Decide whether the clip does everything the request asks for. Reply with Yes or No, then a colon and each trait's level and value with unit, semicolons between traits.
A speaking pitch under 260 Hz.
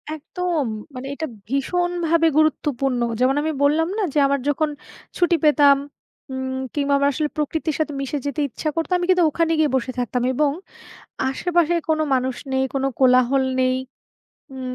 No: very high, 290 Hz